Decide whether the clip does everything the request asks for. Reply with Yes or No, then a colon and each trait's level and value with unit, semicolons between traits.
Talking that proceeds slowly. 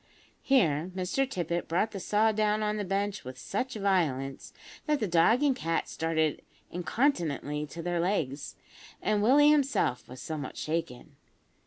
No: average, 150 wpm